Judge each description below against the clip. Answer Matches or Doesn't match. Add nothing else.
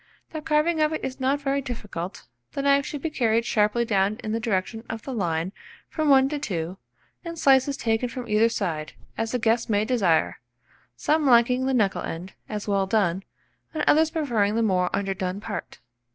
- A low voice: Doesn't match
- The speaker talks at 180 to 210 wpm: Matches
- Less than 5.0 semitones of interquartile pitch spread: Doesn't match